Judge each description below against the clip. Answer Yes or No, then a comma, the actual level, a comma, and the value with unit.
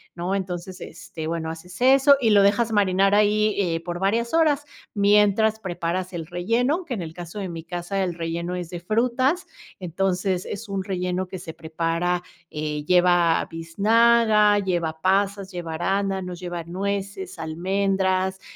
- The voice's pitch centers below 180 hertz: No, medium, 185 Hz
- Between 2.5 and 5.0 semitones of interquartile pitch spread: Yes, average, 3.0 semitones